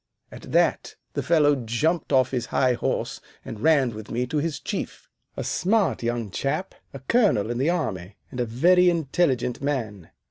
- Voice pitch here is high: No, low, 130 Hz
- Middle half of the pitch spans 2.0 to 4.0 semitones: No, wide, 5.4 semitones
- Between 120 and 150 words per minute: No, average, 175 wpm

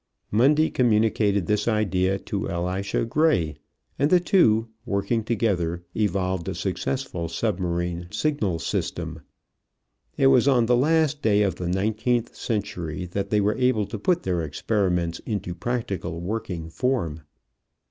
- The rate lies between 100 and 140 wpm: Yes, slow, 135 wpm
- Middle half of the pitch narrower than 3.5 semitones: No, average, 5.0 semitones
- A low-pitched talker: Yes, low, 105 Hz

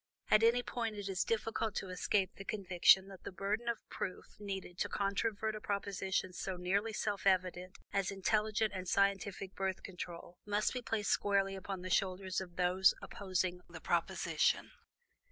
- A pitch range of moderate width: No, narrow, 2.1 semitones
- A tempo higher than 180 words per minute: No, average, 165 wpm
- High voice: Yes, high, 195 Hz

